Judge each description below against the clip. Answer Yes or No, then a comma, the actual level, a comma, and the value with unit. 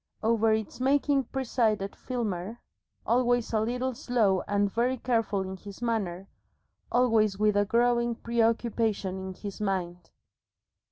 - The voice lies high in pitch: Yes, high, 225 Hz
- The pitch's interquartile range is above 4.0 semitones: No, average, 3.4 semitones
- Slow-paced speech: Yes, slow, 125 wpm